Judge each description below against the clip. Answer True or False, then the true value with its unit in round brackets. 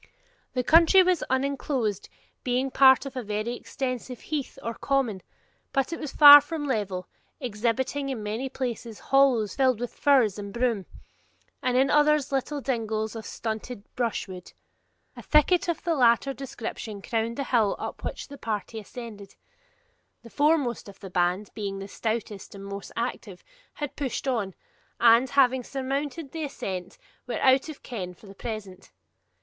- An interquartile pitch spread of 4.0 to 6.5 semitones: True (4.4 semitones)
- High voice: True (245 Hz)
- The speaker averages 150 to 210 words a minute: True (155 wpm)